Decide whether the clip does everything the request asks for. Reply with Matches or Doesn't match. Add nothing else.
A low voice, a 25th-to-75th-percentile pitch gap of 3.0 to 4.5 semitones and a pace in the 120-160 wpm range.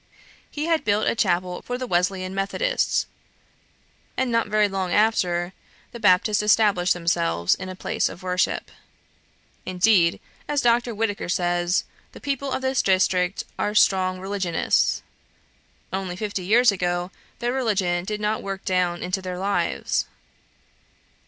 Doesn't match